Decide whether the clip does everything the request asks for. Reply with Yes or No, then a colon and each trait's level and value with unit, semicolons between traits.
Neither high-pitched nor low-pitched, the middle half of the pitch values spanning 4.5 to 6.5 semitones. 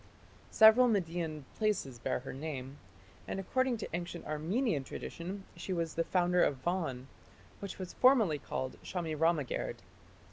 Yes: medium, 170 Hz; average, 4.8 semitones